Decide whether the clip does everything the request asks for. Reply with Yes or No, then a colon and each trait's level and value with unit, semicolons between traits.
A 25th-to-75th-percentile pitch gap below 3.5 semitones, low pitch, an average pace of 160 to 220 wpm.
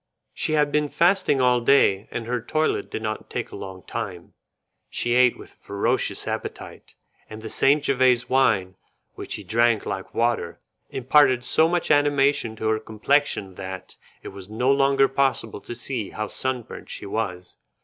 No: average, 4.3 semitones; low, 120 Hz; average, 170 wpm